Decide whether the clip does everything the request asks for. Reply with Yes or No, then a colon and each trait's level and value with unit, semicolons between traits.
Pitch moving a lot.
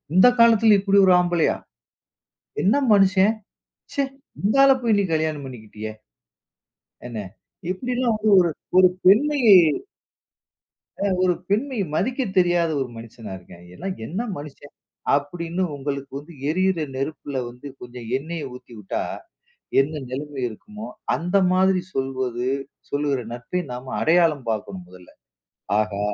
Yes: wide, 6.9 semitones